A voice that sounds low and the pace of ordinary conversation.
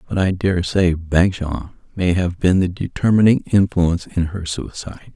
Yes: very low, 90 Hz; average, 165 wpm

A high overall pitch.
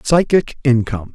No: low, 135 Hz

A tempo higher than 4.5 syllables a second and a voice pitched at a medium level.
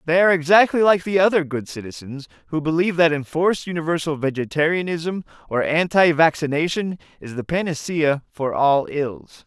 Yes: 5.4 syllables/s; medium, 160 Hz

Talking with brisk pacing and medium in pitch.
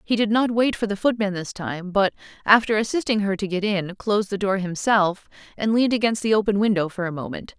No: fast, 230 wpm; high, 205 Hz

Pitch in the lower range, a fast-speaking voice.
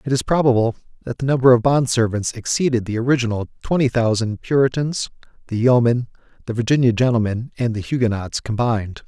No: low, 120 Hz; average, 160 wpm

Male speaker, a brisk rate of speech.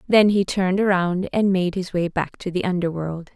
No: female; fast, 215 wpm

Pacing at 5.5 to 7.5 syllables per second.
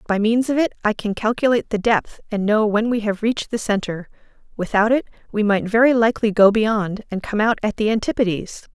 Yes: 5.7 syllables/s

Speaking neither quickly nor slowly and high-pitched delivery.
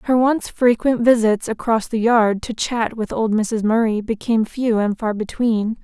Yes: average, 185 wpm; high, 225 Hz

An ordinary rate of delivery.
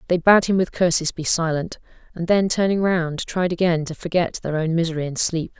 No: fast, 215 wpm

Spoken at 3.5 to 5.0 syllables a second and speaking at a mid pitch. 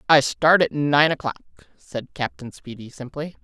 Yes: 4.6 syllables/s; medium, 145 Hz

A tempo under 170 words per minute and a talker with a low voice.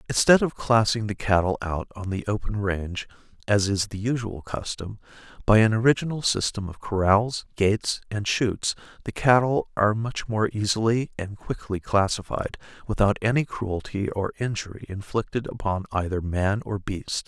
Yes: average, 155 wpm; low, 105 Hz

